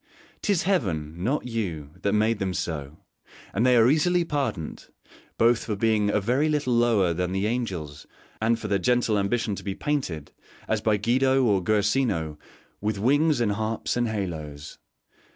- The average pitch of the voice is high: No, low, 110 Hz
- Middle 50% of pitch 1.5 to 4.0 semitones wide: No, average, 4.8 semitones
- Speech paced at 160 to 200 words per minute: Yes, average, 165 wpm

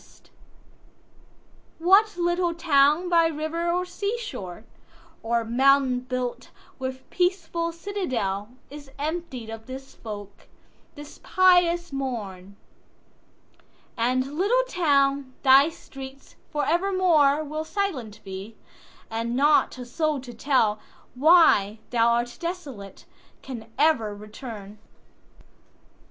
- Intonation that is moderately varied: No, wide, 6.3 semitones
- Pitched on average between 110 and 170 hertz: No, very high, 275 Hz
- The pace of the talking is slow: Yes, slow, 90 wpm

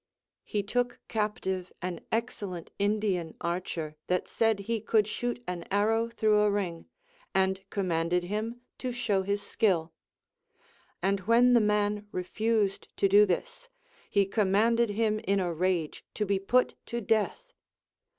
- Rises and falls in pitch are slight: No, average, 3.1 semitones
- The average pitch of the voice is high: Yes, high, 205 Hz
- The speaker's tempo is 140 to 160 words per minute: Yes, average, 145 wpm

